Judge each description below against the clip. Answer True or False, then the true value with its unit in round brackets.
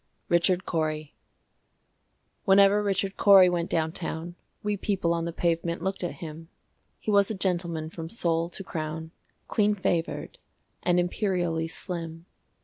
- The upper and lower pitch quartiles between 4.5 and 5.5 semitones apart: False (2.8 semitones)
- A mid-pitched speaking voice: True (175 Hz)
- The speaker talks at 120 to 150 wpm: True (140 wpm)